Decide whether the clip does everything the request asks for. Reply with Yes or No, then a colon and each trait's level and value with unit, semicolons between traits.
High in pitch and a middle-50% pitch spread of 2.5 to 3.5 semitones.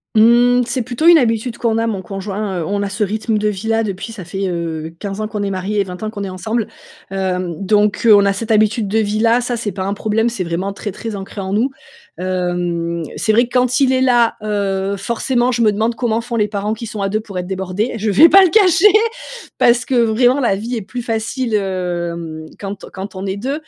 Yes: high, 210 Hz; average, 3.2 semitones